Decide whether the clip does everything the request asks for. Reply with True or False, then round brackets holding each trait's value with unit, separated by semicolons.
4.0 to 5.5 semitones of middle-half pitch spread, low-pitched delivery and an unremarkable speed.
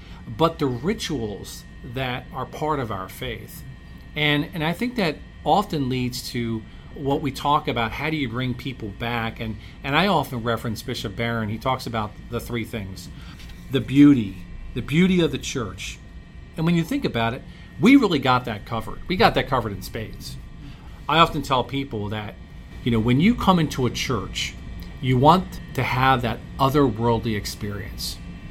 True (4.9 semitones; 125 Hz; 175 wpm)